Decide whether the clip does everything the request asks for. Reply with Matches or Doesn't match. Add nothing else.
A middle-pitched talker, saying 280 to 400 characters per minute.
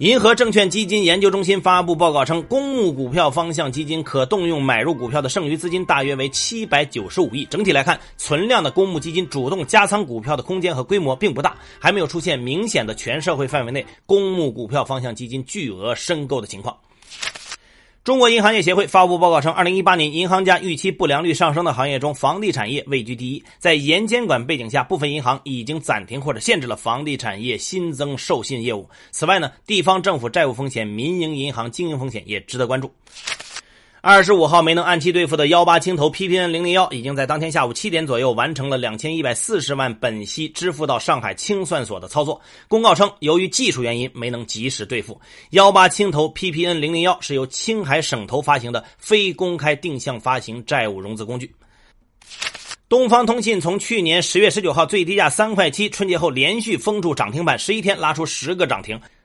Matches